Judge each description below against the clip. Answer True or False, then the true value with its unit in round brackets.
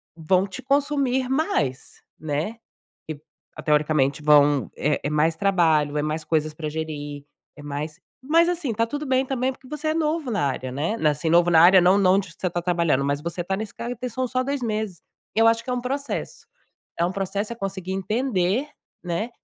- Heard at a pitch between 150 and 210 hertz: True (185 Hz)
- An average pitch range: False (8.2 semitones)